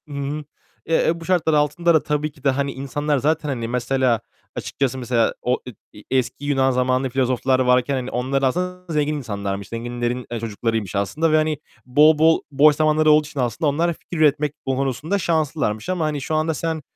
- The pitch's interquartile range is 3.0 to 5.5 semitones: Yes, average, 3.6 semitones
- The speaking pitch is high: No, medium, 140 Hz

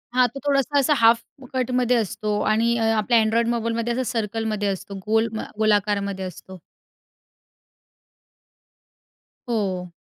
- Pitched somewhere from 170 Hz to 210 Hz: No, high, 225 Hz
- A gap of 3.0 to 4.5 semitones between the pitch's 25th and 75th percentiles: No, narrow, 2.4 semitones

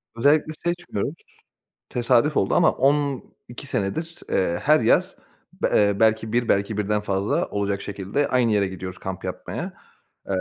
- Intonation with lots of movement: Yes, wide, 6.1 semitones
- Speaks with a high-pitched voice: No, low, 110 Hz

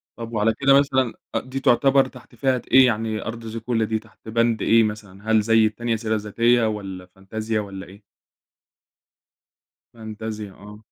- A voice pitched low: Yes, low, 110 Hz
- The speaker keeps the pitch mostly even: Yes, narrow, 1.9 semitones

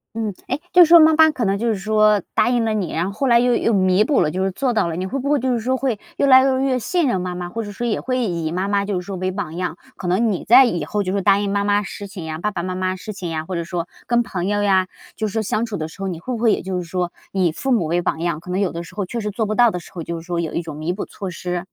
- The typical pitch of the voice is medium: No, high, 200 Hz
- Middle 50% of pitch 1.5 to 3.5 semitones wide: No, average, 4.4 semitones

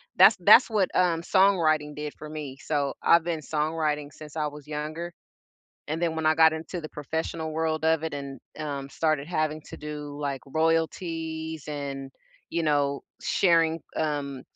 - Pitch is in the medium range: Yes, medium, 155 Hz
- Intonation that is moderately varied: No, narrow, 1.6 semitones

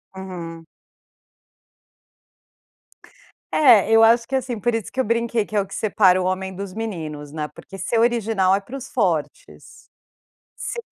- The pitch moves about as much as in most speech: Yes, average, 3.9 semitones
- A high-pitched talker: Yes, high, 205 Hz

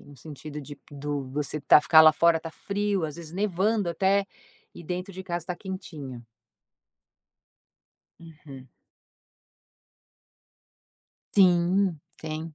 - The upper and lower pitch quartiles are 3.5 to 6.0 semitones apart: Yes, average, 3.9 semitones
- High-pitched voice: No, medium, 165 Hz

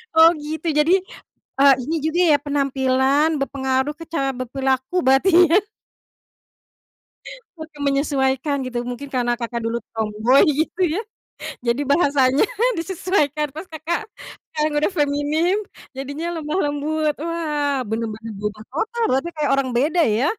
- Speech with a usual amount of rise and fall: Yes, average, 3.2 semitones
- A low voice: No, very high, 285 Hz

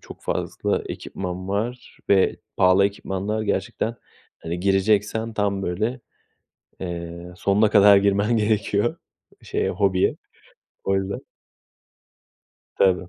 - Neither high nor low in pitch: No, low, 100 Hz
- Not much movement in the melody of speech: Yes, narrow, 2.3 semitones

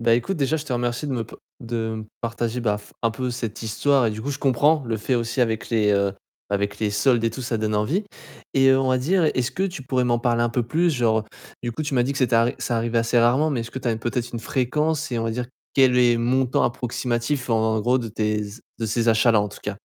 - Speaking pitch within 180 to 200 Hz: No, low, 120 Hz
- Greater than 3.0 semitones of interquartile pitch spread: No, narrow, 2.6 semitones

